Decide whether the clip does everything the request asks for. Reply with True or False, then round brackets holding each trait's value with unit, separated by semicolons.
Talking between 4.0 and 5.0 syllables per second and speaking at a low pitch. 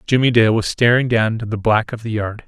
False (6.0 syllables/s; 115 Hz)